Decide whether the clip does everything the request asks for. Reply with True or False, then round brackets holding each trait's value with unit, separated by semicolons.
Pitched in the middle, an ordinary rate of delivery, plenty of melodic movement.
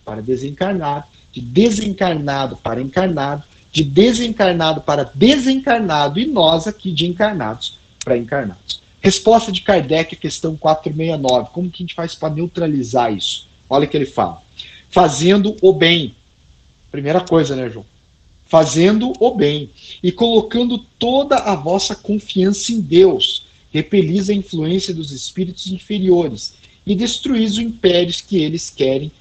True (170 Hz; 135 wpm; 6.5 semitones)